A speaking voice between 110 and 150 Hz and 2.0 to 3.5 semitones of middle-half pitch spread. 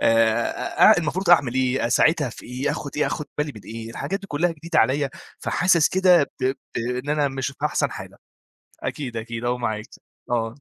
No: low, 135 Hz; average, 4.2 semitones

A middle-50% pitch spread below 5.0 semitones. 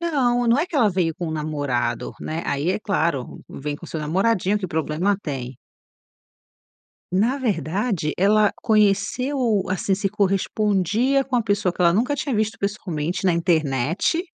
No: wide, 5.4 semitones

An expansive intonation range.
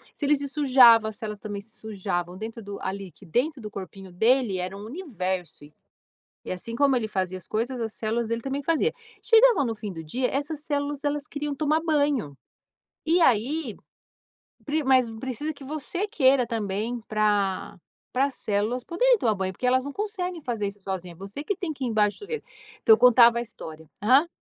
Yes: wide, 6.0 semitones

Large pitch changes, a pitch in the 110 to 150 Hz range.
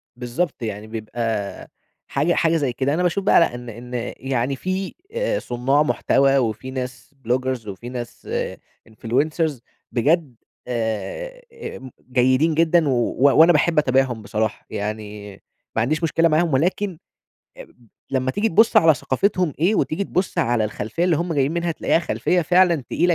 Yes: wide, 5.7 semitones; low, 135 Hz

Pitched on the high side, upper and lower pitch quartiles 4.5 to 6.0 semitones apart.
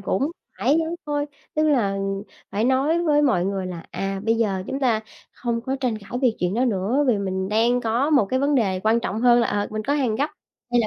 Yes: high, 230 Hz; average, 5.1 semitones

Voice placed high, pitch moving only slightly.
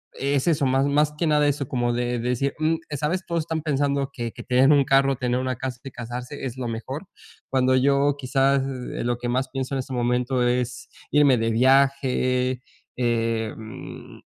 No: low, 130 Hz; narrow, 2.3 semitones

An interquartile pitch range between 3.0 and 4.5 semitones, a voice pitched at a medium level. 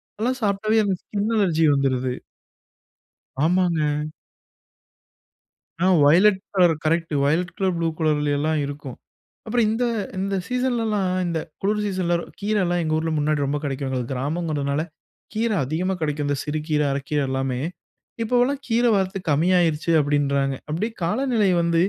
No: wide, 5.5 semitones; medium, 170 Hz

